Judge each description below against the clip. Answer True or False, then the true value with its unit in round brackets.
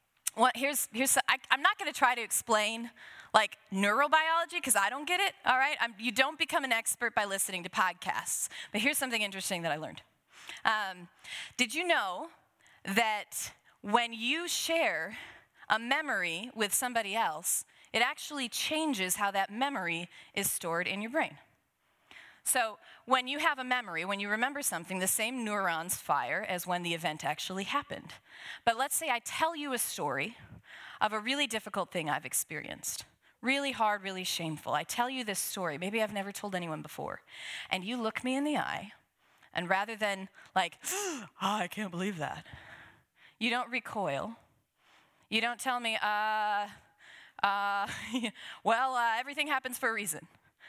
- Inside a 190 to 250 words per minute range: False (170 wpm)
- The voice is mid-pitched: False (225 Hz)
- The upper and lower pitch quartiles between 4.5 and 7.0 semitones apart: True (5.3 semitones)